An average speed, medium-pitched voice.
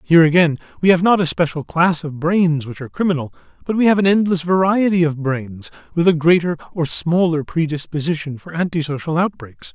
Yes: average, 185 wpm; medium, 165 Hz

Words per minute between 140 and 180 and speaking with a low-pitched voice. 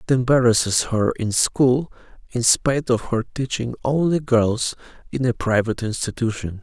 Yes: average, 145 wpm; low, 120 Hz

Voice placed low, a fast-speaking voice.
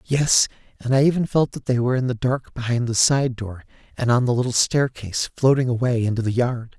Yes: low, 125 Hz; fast, 220 wpm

